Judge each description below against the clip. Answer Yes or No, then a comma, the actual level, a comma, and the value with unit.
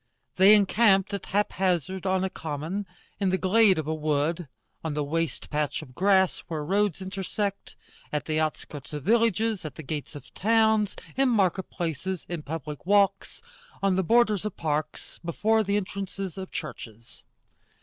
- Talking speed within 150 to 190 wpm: Yes, average, 160 wpm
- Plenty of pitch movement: No, average, 4.5 semitones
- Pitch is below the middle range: No, medium, 185 Hz